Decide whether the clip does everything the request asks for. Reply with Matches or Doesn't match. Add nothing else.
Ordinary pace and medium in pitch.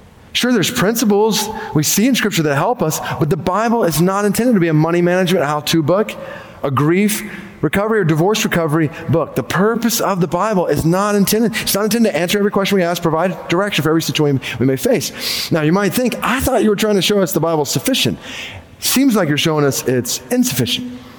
Doesn't match